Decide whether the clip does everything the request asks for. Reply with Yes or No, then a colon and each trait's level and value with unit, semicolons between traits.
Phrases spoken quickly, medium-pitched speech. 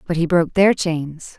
Yes: fast, 215 wpm; medium, 165 Hz